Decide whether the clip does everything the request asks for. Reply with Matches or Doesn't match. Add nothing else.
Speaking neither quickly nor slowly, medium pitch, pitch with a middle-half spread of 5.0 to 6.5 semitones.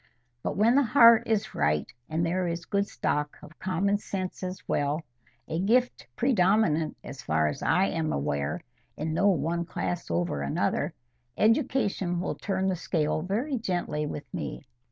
Matches